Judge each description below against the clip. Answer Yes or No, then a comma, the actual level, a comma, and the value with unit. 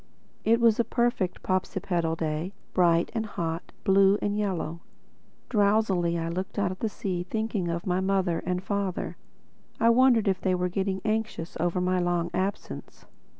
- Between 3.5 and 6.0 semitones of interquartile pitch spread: No, average, 3.0 semitones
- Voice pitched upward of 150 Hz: Yes, high, 190 Hz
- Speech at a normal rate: Yes, average, 155 wpm